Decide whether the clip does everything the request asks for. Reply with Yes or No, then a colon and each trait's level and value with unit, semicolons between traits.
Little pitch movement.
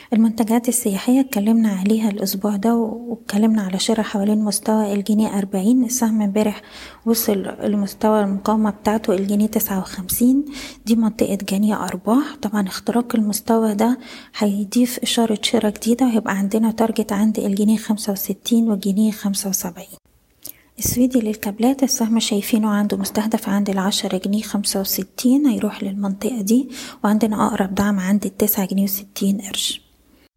Yes: narrow, 2.1 semitones